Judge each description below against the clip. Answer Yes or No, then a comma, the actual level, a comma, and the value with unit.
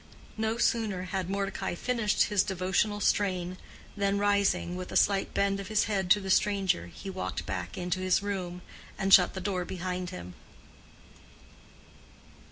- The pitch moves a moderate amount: No, narrow, 2.0 semitones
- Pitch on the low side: No, high, 190 Hz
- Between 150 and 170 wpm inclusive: Yes, average, 155 wpm